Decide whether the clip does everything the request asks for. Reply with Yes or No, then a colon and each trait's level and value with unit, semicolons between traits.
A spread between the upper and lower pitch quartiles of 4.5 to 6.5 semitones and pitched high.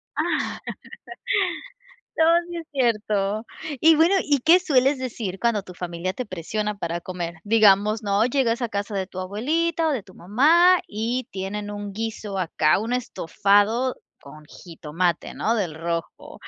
Yes: average, 5.2 semitones; high, 210 Hz